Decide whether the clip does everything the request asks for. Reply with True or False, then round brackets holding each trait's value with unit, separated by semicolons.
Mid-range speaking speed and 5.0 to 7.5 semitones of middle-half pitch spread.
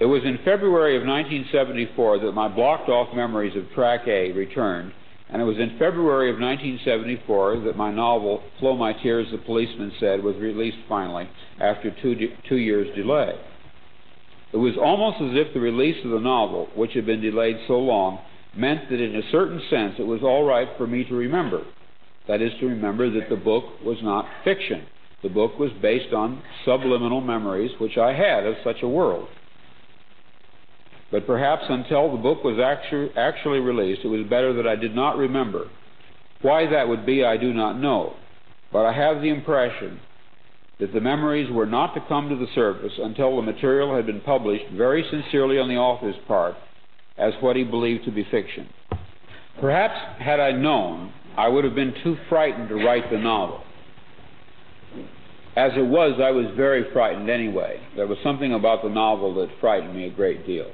False (185 wpm; 3.5 semitones)